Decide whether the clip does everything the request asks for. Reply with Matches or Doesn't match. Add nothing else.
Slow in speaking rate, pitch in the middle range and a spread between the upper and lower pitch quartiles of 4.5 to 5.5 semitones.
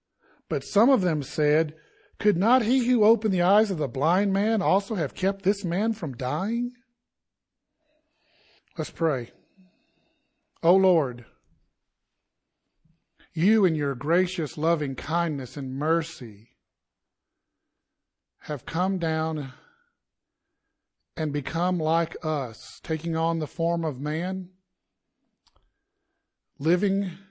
Matches